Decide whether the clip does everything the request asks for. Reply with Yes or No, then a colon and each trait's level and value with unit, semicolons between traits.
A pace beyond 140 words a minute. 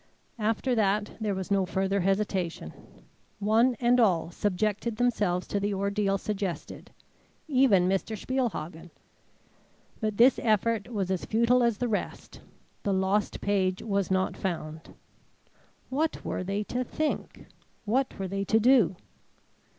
No: slow, 135 wpm